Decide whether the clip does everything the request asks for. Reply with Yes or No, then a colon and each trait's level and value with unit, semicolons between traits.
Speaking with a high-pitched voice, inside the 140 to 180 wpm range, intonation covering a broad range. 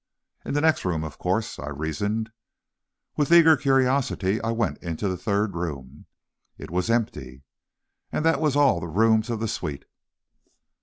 No: low, 105 Hz; average, 165 wpm; wide, 7.8 semitones